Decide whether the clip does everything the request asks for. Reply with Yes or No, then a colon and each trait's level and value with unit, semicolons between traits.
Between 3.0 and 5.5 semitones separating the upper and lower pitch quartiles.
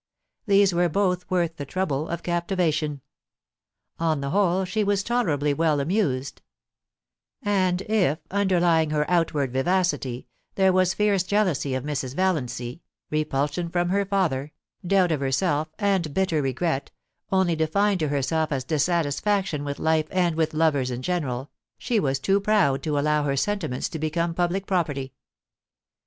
Yes: average, 4.5 semitones